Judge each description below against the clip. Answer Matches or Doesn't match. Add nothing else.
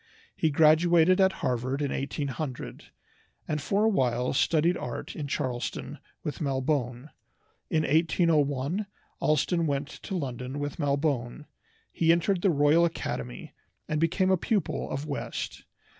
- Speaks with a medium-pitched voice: Matches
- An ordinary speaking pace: Doesn't match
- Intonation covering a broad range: Doesn't match